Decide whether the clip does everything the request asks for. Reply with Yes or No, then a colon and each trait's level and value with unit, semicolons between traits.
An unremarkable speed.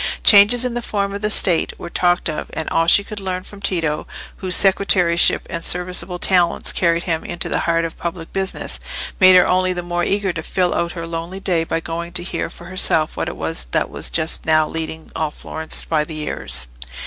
No: fast, 215 wpm